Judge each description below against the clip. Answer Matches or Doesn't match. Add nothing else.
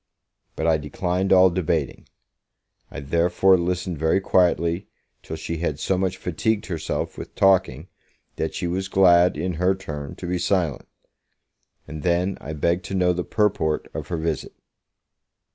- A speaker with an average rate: Matches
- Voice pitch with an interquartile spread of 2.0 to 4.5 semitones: Matches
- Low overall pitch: Matches